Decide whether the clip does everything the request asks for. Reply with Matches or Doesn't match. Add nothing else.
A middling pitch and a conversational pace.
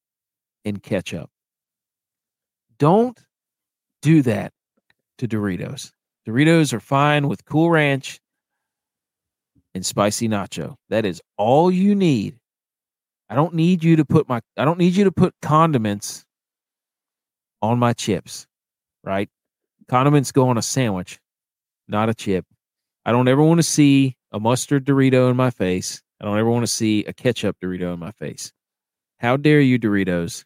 Doesn't match